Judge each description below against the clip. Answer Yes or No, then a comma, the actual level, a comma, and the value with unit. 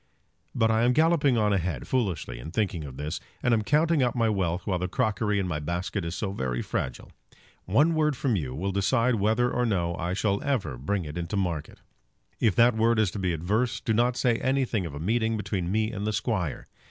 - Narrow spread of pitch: No, average, 5.2 semitones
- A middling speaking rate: No, fast, 225 wpm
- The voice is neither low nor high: No, low, 105 Hz